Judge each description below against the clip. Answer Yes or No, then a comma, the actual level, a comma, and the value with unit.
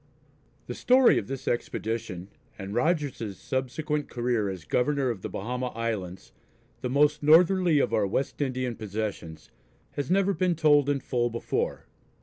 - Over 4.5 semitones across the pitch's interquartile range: Yes, wide, 5.5 semitones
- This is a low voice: Yes, low, 125 Hz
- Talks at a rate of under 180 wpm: Yes, average, 145 wpm